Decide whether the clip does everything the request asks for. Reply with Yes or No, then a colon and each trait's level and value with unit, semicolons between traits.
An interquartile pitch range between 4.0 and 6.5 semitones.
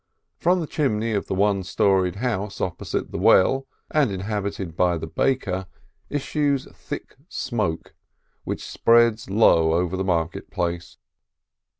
Yes: average, 4.7 semitones